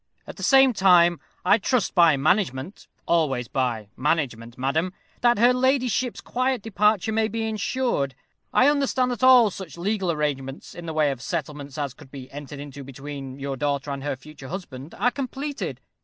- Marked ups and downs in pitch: Yes, wide, 8.3 semitones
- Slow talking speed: No, average, 170 wpm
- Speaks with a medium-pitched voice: Yes, medium, 165 Hz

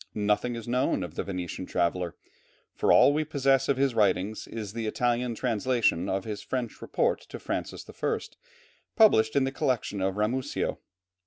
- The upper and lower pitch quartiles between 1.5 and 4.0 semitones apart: No, average, 4.7 semitones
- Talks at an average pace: Yes, average, 160 wpm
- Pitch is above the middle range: No, low, 115 Hz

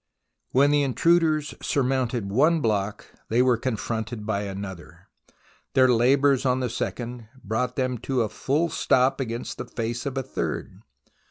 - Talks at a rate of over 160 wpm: No, average, 150 wpm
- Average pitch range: Yes, average, 3.2 semitones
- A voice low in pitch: Yes, low, 125 Hz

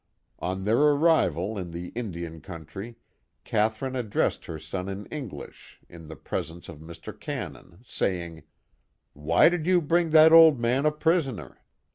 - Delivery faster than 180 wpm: No, average, 155 wpm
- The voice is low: Yes, low, 105 Hz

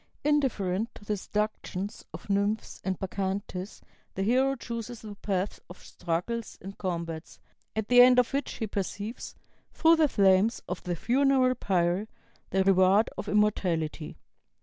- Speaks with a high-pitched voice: Yes, high, 205 Hz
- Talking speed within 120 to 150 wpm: Yes, average, 145 wpm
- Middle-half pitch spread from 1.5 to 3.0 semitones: No, average, 3.9 semitones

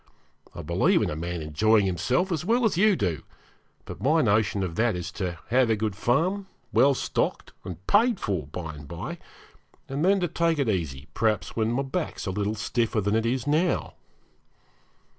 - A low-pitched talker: Yes, low, 110 Hz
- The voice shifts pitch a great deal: Yes, wide, 8.9 semitones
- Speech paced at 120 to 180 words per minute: No, average, 195 wpm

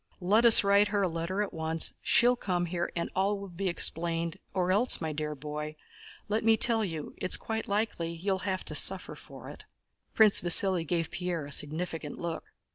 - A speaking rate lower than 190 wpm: No, average, 200 wpm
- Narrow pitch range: No, average, 3.5 semitones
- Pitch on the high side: No, medium, 180 Hz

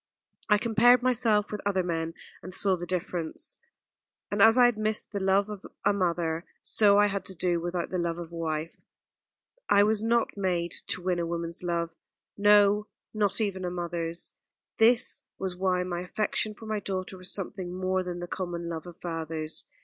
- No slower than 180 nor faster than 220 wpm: Yes, average, 190 wpm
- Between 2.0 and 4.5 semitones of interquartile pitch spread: Yes, average, 3.2 semitones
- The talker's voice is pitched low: No, medium, 185 Hz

